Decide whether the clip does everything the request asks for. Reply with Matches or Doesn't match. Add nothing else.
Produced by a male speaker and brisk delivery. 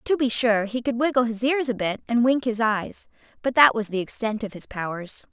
Doesn't match